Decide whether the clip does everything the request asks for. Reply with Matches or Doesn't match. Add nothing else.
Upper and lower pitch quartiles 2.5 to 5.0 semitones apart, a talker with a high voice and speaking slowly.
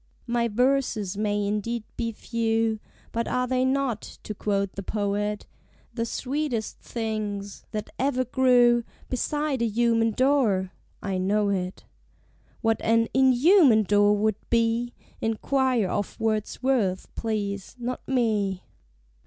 Matches